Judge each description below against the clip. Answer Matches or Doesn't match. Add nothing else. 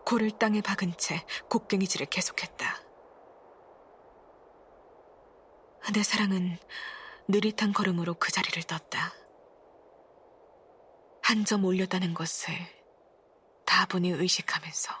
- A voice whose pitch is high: Matches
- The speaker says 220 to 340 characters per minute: Doesn't match